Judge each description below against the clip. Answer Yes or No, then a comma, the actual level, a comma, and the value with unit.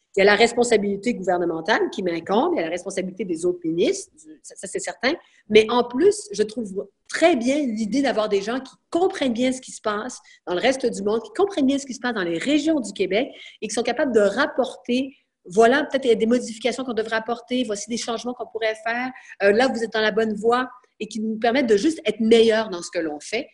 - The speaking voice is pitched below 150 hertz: No, high, 235 Hz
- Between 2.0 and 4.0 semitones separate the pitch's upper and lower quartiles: Yes, average, 3.6 semitones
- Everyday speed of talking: No, fast, 250 wpm